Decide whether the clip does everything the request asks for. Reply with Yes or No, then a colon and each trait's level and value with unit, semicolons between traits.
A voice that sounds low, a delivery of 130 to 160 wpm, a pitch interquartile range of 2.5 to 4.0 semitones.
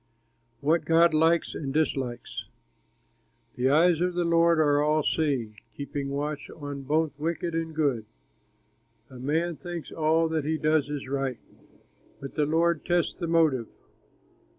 No: medium, 155 Hz; average, 145 wpm; average, 2.8 semitones